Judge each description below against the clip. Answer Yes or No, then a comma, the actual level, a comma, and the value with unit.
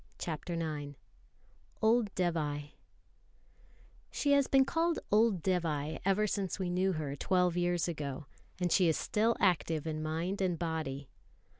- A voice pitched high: No, medium, 175 Hz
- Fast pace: No, average, 140 wpm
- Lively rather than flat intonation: No, average, 3.9 semitones